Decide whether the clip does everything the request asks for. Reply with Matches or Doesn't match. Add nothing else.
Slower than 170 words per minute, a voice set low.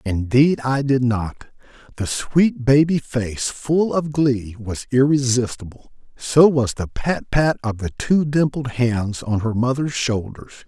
Matches